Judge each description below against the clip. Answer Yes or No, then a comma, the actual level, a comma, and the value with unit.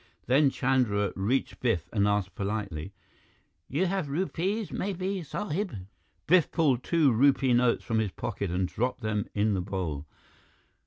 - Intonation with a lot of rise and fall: Yes, wide, 7.4 semitones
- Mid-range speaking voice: No, low, 125 Hz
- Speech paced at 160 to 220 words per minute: No, average, 145 wpm